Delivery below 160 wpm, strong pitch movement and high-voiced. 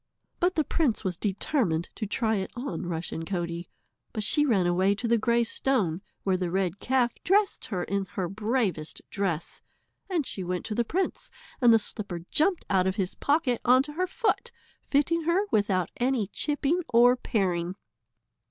No: average, 175 wpm; wide, 6.6 semitones; high, 220 Hz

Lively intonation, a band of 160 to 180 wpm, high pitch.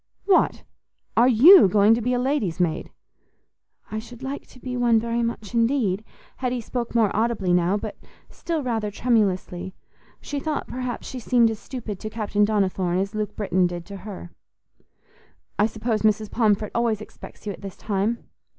No: average, 3.3 semitones; average, 170 wpm; high, 220 Hz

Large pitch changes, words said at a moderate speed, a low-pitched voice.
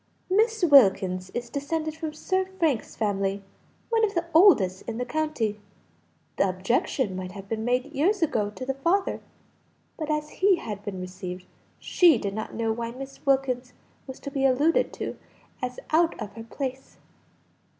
No: wide, 7.2 semitones; average, 165 wpm; very high, 255 Hz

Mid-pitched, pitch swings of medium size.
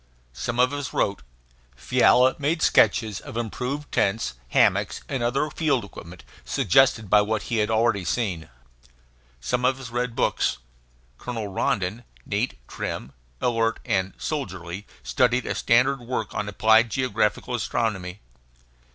No: low, 115 Hz; average, 3.7 semitones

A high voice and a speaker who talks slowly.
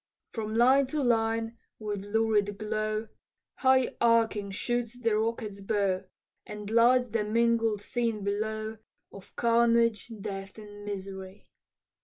Yes: high, 220 Hz; slow, 120 wpm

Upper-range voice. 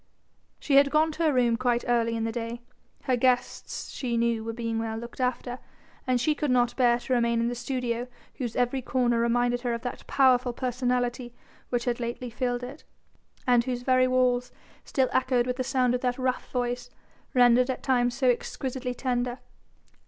Yes: high, 245 Hz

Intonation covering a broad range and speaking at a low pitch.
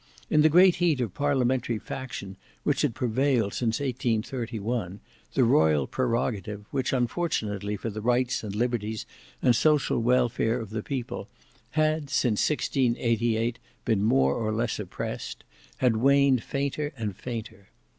No: average, 3.6 semitones; low, 120 Hz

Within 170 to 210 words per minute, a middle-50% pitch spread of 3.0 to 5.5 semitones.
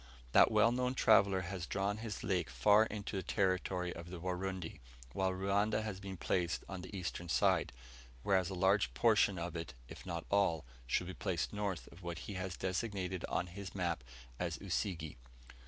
No: average, 180 wpm; narrow, 2.5 semitones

